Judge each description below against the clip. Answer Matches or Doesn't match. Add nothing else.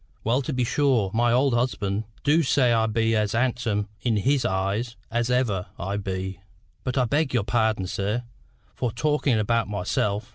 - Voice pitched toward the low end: Matches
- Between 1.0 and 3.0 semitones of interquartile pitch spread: Doesn't match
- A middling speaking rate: Matches